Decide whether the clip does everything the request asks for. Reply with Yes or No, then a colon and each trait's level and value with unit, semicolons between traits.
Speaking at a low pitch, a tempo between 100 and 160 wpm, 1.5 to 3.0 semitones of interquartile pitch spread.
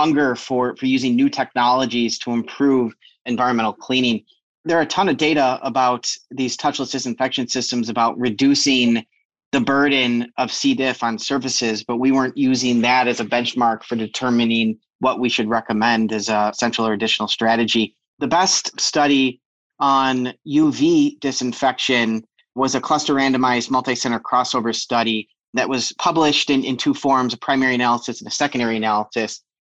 Yes: low, 125 Hz; average, 155 wpm; narrow, 2.5 semitones